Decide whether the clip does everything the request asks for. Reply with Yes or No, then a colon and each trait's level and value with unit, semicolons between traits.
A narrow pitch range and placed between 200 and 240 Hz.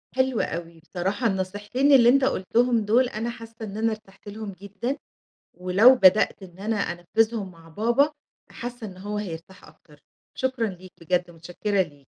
No: average, 4.3 semitones; high, 205 Hz